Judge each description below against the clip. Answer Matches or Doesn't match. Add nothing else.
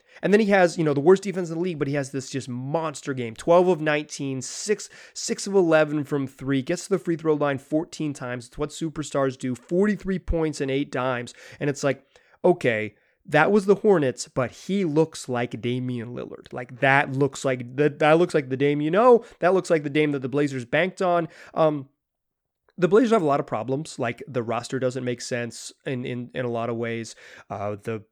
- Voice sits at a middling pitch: Matches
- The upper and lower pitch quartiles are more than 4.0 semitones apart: Matches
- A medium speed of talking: Doesn't match